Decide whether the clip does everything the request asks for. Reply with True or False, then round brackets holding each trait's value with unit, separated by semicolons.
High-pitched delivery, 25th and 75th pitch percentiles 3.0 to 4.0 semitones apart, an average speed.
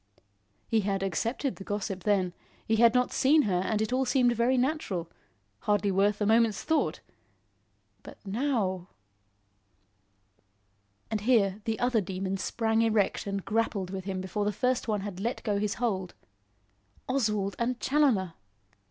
True (210 Hz; 3.6 semitones; 150 wpm)